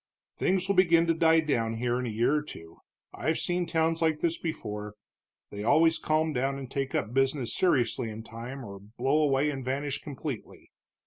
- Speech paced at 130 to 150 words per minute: No, average, 190 wpm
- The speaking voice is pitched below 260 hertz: Yes, low, 135 Hz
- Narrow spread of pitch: No, average, 5.3 semitones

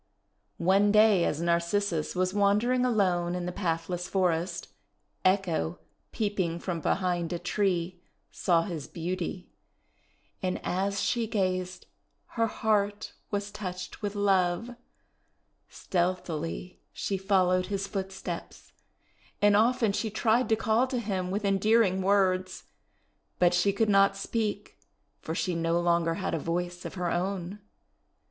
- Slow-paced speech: Yes, slow, 130 wpm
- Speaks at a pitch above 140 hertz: Yes, medium, 185 Hz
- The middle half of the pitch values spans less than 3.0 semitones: Yes, narrow, 2.6 semitones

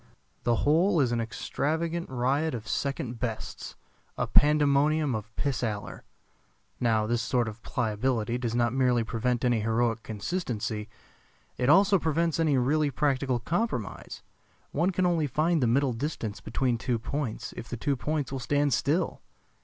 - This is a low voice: Yes, low, 130 Hz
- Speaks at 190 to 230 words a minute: No, average, 155 wpm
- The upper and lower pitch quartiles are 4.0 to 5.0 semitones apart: Yes, average, 4.6 semitones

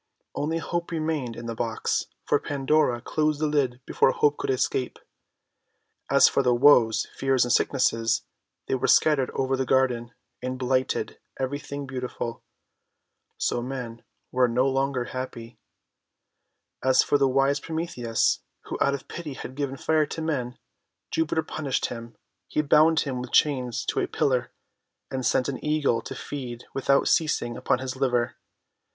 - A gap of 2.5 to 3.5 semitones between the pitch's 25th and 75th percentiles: Yes, average, 2.8 semitones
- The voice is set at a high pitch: No, low, 130 Hz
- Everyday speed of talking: Yes, average, 155 wpm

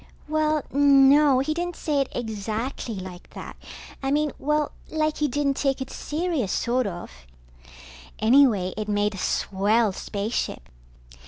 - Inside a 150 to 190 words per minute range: No, average, 140 wpm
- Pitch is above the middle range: Yes, very high, 265 Hz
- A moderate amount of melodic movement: No, wide, 5.9 semitones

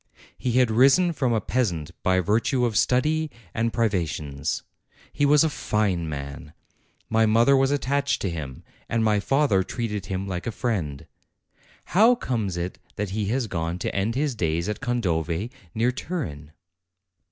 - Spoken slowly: No, average, 160 wpm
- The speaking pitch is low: Yes, low, 110 Hz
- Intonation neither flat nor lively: No, wide, 6.4 semitones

